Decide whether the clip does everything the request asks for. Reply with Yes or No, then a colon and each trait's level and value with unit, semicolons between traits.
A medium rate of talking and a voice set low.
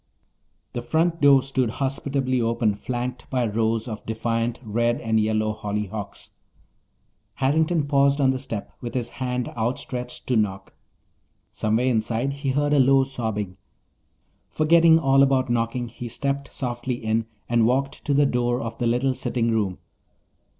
Yes: average, 150 wpm; low, 120 Hz